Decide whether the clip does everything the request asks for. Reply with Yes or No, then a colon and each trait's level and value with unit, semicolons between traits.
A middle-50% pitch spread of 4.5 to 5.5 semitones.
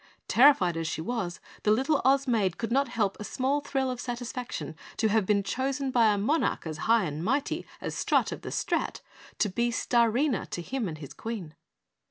Yes: average, 5.2 semitones